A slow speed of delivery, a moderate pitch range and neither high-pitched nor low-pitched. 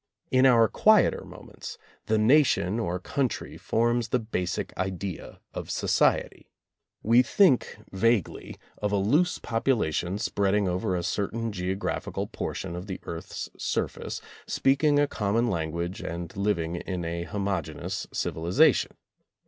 No: slow, 130 wpm; average, 4.6 semitones; low, 100 Hz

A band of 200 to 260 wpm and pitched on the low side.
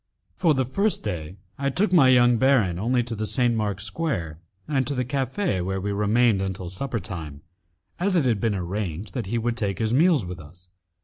Yes: fast, 205 wpm; low, 115 Hz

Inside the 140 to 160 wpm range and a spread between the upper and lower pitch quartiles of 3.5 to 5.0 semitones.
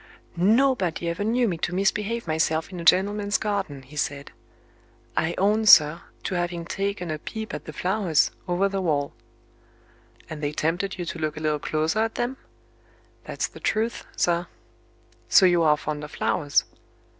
No: average, 170 wpm; average, 4.5 semitones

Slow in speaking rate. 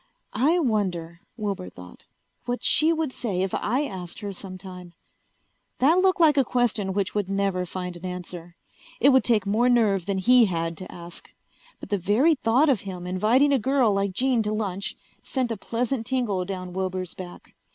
No: average, 185 wpm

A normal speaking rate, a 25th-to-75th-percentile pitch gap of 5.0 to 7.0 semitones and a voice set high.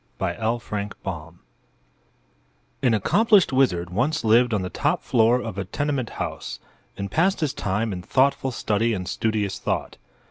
No: average, 150 wpm; wide, 5.4 semitones; low, 115 Hz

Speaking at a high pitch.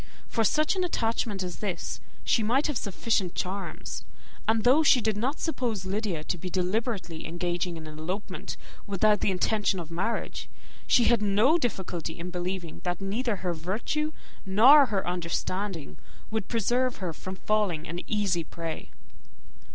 Yes: high, 195 Hz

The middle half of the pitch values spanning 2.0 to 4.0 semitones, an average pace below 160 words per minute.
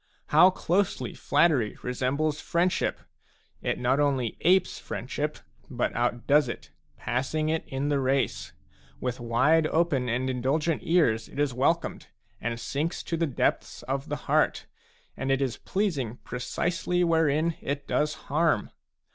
No: average, 4.4 semitones; average, 140 wpm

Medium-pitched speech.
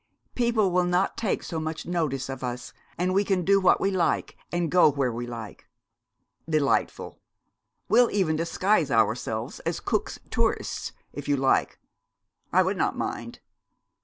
Yes: medium, 165 Hz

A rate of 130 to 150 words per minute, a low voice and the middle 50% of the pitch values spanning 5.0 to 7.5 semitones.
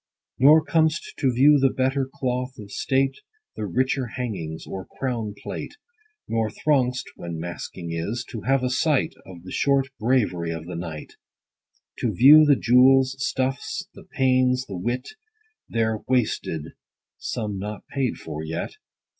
Yes: average, 145 wpm; low, 125 Hz; wide, 5.5 semitones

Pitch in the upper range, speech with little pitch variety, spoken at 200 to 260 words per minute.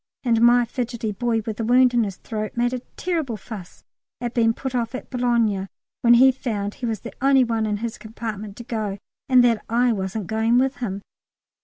Yes: high, 230 Hz; narrow, 2.3 semitones; fast, 205 wpm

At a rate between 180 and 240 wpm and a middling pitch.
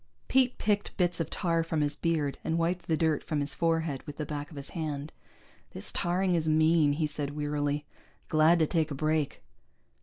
Yes: average, 200 wpm; medium, 155 Hz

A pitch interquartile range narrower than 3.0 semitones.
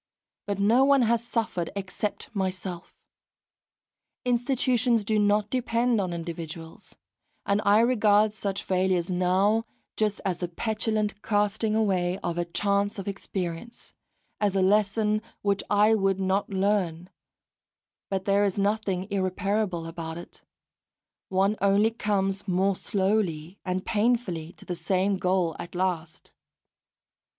Yes: narrow, 2.6 semitones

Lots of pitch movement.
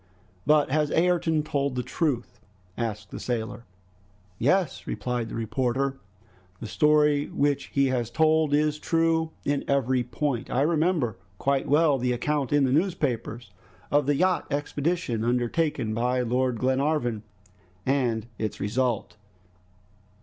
No: average, 3.8 semitones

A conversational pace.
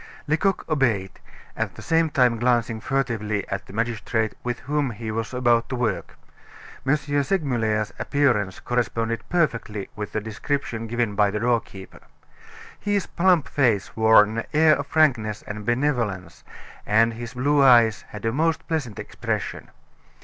Yes: average, 145 wpm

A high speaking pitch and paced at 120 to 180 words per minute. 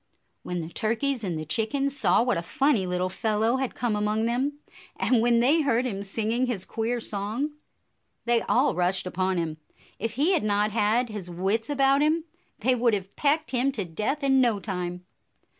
No: high, 225 Hz; average, 190 wpm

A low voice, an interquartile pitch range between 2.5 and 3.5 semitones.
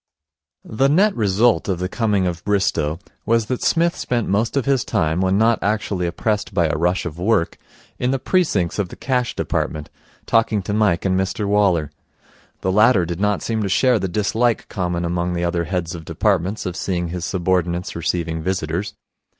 No: very low, 95 Hz; average, 4.1 semitones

